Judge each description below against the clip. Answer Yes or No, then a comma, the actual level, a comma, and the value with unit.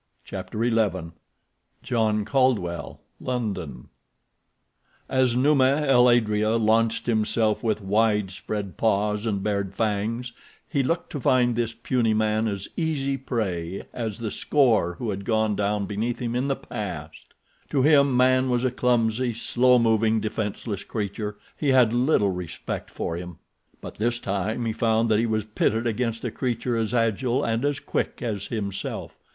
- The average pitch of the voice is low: Yes, low, 115 Hz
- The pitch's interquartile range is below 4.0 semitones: Yes, average, 2.9 semitones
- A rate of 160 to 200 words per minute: No, average, 150 wpm